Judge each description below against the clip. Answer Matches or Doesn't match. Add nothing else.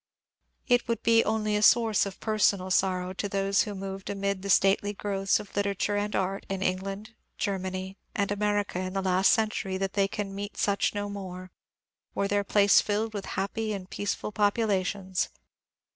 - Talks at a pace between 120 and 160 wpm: Doesn't match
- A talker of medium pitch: Doesn't match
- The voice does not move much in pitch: Matches